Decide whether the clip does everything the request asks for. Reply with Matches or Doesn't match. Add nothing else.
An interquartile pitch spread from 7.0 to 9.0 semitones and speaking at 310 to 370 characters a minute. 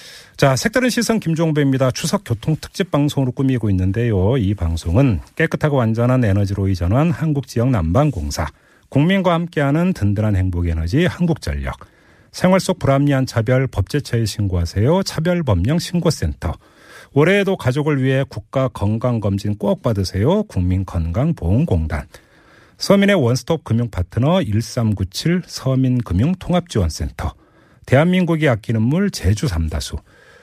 Matches